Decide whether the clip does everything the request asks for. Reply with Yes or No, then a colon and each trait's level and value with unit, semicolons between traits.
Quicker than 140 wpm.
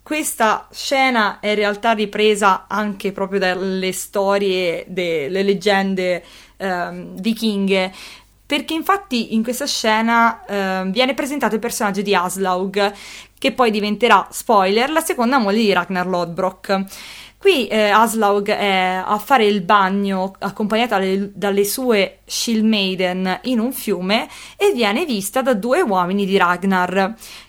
No: average, 130 wpm